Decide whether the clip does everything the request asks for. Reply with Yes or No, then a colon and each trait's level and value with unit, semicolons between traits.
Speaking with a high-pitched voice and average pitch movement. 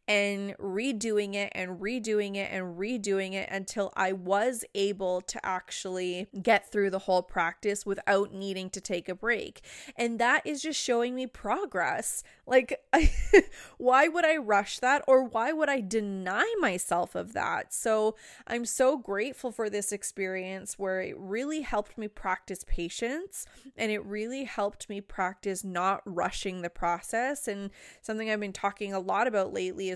Yes: high, 205 Hz; average, 3.9 semitones